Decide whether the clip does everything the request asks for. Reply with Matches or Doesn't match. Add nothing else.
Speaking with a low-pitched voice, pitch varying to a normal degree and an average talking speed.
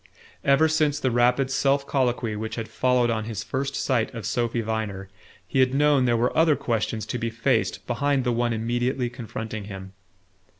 Matches